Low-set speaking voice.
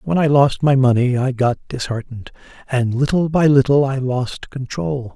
Yes: low, 130 Hz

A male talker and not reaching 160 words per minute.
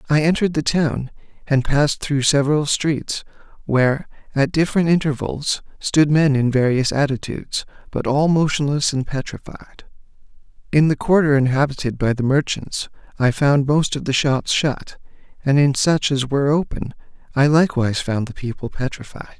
Yes: male; average, 150 wpm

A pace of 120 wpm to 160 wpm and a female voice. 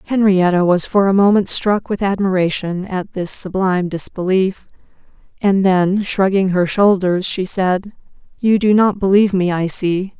Yes: average, 155 wpm; female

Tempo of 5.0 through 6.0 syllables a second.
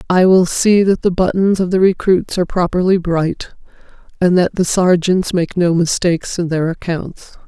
No: 4.7 syllables/s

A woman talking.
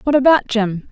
Yes: female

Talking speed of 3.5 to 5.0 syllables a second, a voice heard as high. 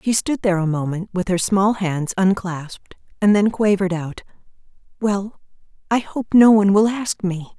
Yes: 4.9 syllables/s; high, 195 Hz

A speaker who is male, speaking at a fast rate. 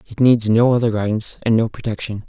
Yes: male; fast, 210 wpm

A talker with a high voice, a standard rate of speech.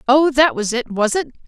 No: very high, 260 Hz; fast, 245 wpm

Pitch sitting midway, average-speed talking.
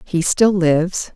Yes: medium, 175 Hz; average, 155 wpm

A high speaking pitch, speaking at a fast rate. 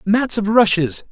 No: high, 205 Hz; average, 160 wpm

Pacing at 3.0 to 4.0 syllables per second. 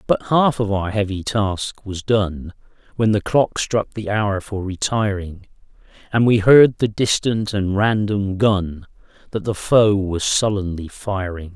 Yes: 3.9 syllables/s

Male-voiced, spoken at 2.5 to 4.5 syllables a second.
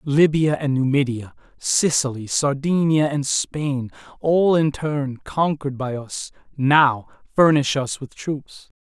Yes: male; 3.7 syllables/s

